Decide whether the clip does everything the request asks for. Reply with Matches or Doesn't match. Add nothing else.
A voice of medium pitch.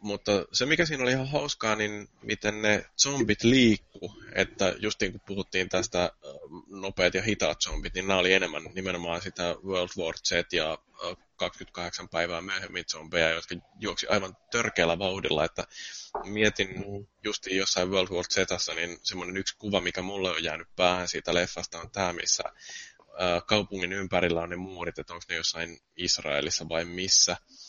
Doesn't match